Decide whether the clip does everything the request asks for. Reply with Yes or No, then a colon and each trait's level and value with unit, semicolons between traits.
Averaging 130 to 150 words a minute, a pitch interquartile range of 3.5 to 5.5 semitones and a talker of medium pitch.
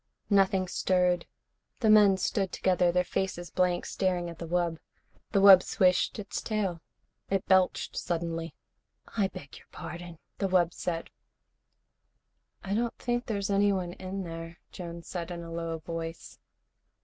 No: average, 145 wpm; narrow, 2.4 semitones; medium, 180 Hz